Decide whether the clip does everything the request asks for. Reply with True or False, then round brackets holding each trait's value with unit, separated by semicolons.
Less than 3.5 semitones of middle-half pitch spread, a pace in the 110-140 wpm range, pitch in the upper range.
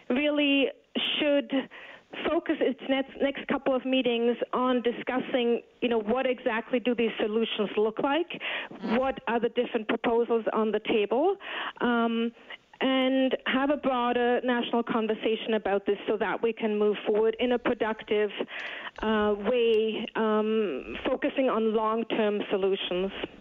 True (2.9 semitones; 135 wpm; 240 Hz)